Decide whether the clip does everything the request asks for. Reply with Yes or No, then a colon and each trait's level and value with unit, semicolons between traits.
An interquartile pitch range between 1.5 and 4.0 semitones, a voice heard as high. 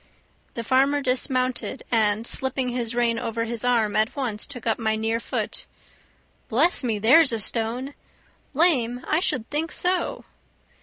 Yes: average, 2.9 semitones; high, 245 Hz